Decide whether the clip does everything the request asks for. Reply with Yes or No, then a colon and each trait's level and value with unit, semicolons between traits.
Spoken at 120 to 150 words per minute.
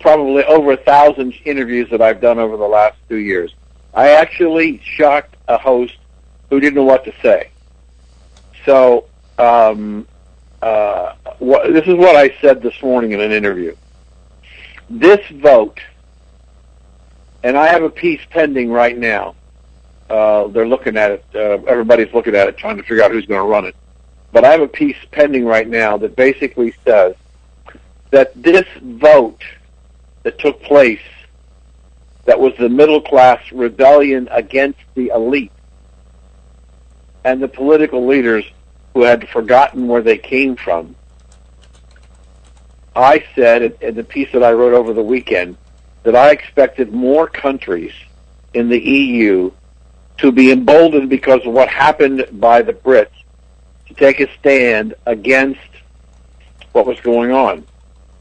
Yes: average, 145 wpm